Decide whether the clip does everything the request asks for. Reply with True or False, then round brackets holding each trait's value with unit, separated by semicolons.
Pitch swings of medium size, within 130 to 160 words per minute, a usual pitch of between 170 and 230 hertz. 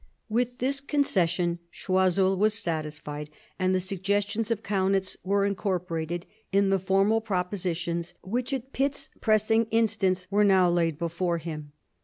True (3.7 semitones; 140 wpm; 190 Hz)